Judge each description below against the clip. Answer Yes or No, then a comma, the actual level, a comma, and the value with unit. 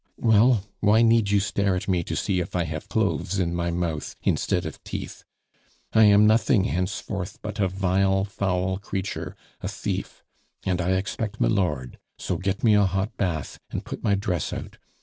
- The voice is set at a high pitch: No, very low, 95 Hz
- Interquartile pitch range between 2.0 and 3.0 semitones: Yes, narrow, 2.4 semitones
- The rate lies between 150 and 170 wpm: No, average, 180 wpm